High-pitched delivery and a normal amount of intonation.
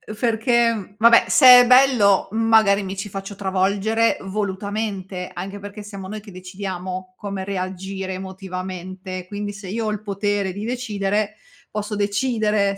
No: high, 200 Hz; narrow, 2.1 semitones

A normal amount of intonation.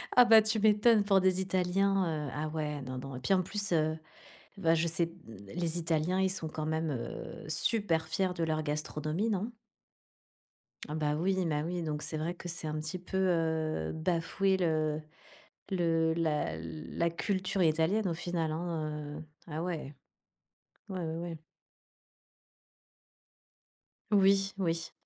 Yes: average, 3.3 semitones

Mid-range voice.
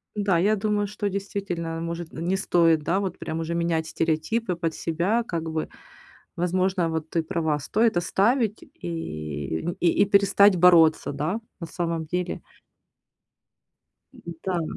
Yes: medium, 170 Hz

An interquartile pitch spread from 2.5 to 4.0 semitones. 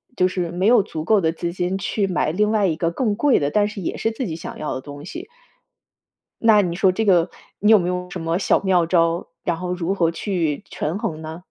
Yes: average, 3.7 semitones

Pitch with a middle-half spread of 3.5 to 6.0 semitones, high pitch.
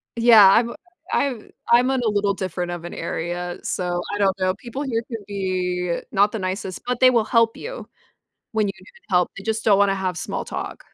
Yes: average, 3.9 semitones; high, 200 Hz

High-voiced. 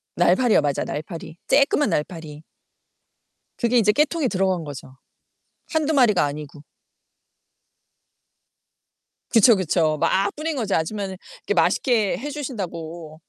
Yes: high, 195 Hz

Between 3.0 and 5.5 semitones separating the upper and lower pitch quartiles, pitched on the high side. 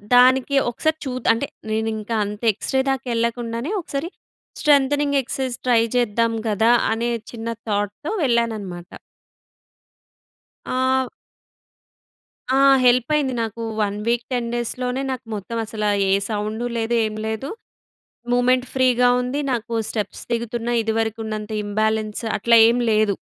No: narrow, 2.5 semitones; high, 235 Hz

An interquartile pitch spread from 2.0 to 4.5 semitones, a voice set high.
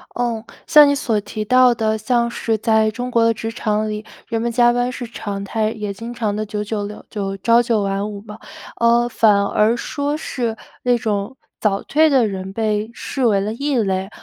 Yes: narrow, 2.4 semitones; high, 225 Hz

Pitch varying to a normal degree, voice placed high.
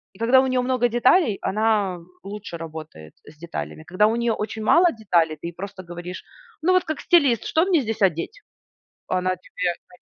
No: wide, 6.4 semitones; high, 210 Hz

